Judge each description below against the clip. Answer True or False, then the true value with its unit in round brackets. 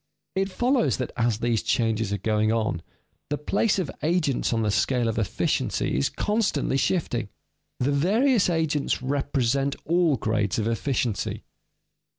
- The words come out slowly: False (150 wpm)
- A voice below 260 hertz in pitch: True (135 Hz)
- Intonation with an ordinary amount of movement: False (6.7 semitones)